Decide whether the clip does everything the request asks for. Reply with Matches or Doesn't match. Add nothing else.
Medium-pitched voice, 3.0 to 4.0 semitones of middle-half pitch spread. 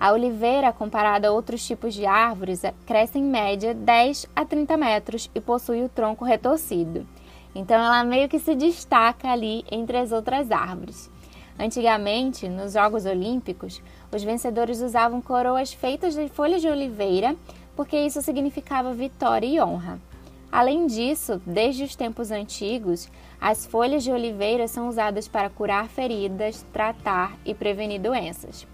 Doesn't match